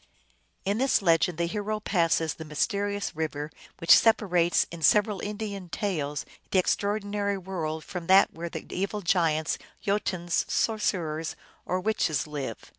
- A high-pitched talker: No, medium, 180 Hz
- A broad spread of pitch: No, average, 4.0 semitones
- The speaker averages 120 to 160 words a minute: Yes, average, 140 wpm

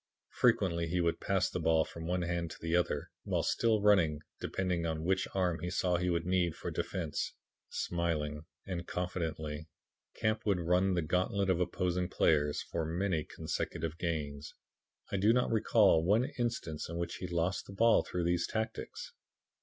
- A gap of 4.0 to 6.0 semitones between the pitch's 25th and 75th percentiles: No, average, 2.7 semitones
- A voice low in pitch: Yes, very low, 90 Hz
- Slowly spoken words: No, average, 170 wpm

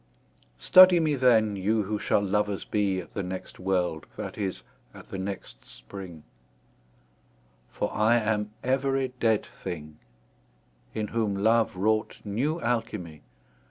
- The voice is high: No, low, 105 Hz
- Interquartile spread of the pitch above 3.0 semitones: Yes, average, 3.4 semitones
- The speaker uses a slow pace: Yes, slow, 130 wpm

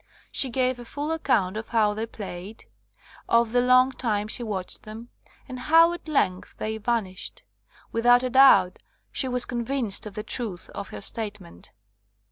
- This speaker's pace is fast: No, average, 165 wpm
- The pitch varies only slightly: No, average, 3.4 semitones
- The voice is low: No, high, 230 Hz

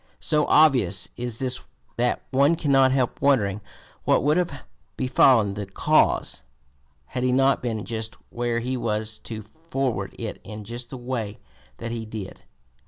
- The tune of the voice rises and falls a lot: No, average, 3.6 semitones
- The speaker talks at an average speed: Yes, average, 155 wpm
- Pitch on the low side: Yes, low, 120 Hz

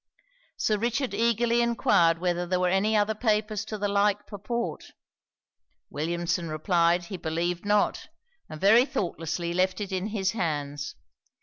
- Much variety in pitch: No, average, 3.9 semitones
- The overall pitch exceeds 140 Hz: Yes, high, 190 Hz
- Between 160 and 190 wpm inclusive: No, average, 140 wpm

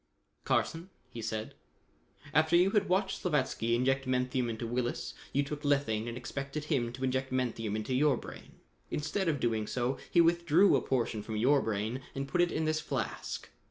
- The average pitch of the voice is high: No, low, 130 Hz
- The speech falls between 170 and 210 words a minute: Yes, average, 180 wpm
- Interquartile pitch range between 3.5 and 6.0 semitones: Yes, average, 4.7 semitones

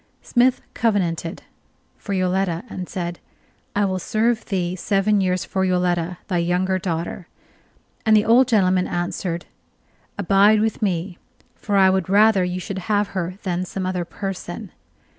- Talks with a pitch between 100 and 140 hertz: No, medium, 185 Hz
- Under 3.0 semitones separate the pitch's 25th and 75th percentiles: Yes, narrow, 2.4 semitones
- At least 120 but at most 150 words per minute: Yes, average, 145 wpm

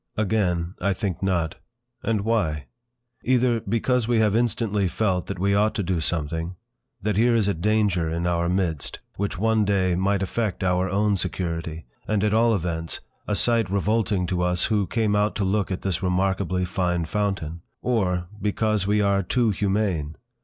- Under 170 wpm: No, average, 175 wpm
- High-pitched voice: No, low, 100 Hz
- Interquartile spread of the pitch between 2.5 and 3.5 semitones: Yes, average, 3.2 semitones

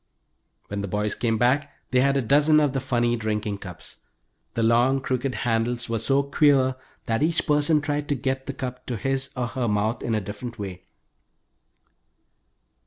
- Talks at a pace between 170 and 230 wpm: Yes, average, 175 wpm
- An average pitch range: Yes, average, 3.5 semitones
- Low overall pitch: Yes, low, 125 Hz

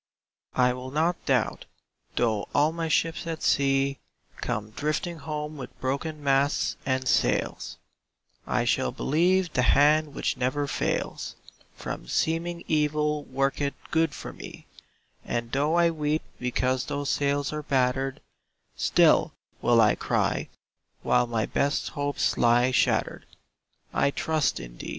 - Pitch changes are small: No, average, 3.2 semitones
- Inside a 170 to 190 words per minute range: No, slow, 135 wpm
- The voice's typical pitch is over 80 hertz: Yes, medium, 140 Hz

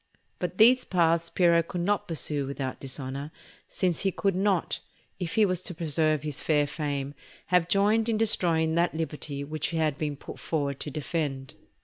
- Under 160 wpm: No, average, 175 wpm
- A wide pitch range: No, average, 3.7 semitones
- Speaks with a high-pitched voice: No, medium, 160 Hz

